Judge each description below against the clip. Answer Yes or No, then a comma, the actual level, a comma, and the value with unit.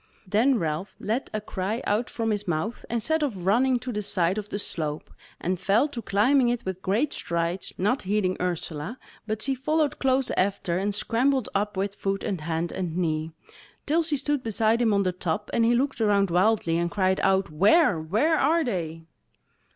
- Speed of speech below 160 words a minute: No, average, 195 wpm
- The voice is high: Yes, high, 205 Hz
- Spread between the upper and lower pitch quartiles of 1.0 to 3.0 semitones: No, average, 4.9 semitones